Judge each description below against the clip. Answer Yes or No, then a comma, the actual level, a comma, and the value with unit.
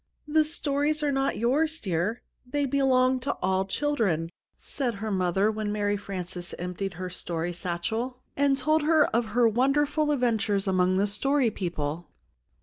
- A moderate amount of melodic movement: No, wide, 7.0 semitones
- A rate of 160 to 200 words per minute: No, average, 145 wpm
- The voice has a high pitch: Yes, high, 220 Hz